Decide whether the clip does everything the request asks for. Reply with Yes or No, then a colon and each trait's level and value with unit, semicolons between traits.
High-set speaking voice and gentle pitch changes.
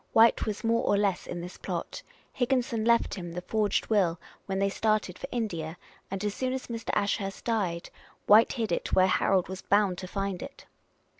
No: high, 200 Hz; average, 3.5 semitones